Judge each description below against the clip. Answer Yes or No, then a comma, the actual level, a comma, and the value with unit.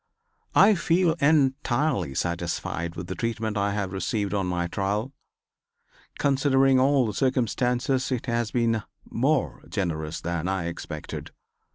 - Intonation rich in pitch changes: Yes, wide, 6.5 semitones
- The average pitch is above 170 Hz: No, low, 115 Hz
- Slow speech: Yes, slow, 130 wpm